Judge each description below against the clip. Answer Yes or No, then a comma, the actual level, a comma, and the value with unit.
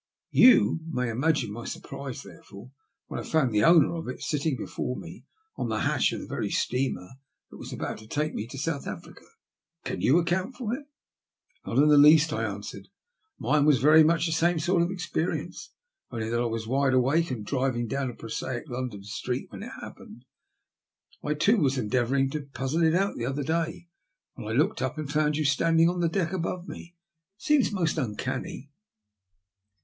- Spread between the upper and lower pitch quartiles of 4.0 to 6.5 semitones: Yes, average, 4.7 semitones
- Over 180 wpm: Yes, average, 195 wpm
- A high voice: No, medium, 145 Hz